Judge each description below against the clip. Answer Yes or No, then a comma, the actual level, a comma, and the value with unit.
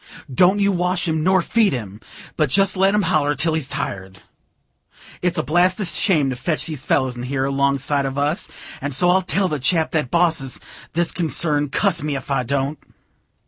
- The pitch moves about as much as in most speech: Yes, average, 4.6 semitones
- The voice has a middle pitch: Yes, medium, 155 Hz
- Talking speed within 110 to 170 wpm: No, average, 195 wpm